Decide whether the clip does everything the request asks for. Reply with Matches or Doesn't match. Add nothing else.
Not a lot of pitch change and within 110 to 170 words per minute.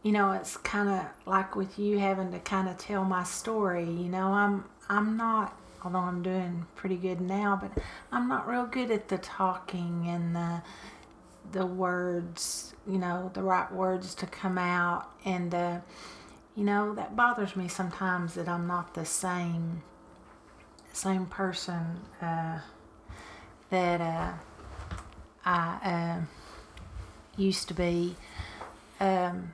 Matches